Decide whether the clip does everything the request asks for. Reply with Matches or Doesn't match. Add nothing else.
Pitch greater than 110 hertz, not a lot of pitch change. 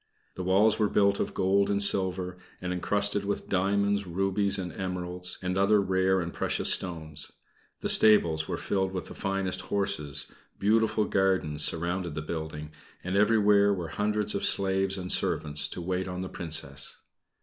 Doesn't match